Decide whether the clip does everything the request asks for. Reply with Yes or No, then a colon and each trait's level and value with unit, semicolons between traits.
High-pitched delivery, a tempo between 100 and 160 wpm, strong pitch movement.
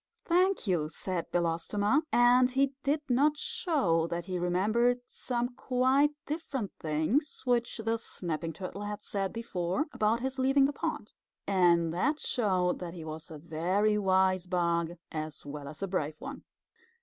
Yes: high, 195 Hz; average, 155 wpm; wide, 6.7 semitones